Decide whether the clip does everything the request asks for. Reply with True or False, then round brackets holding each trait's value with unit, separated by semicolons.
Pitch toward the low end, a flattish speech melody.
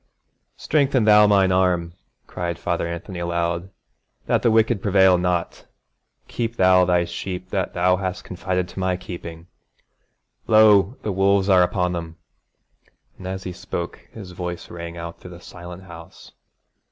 True (90 Hz; 1.9 semitones)